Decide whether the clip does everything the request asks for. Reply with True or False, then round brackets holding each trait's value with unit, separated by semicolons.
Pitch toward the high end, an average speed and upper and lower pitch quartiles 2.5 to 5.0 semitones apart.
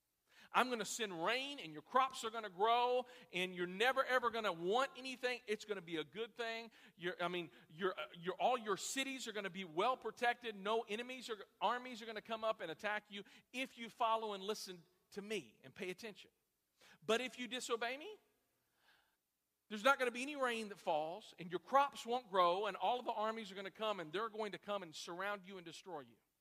False (220 Hz; 230 wpm; 4.3 semitones)